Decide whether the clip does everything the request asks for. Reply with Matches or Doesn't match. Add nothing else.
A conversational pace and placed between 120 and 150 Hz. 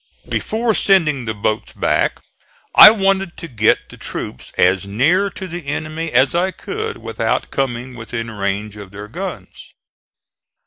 Matches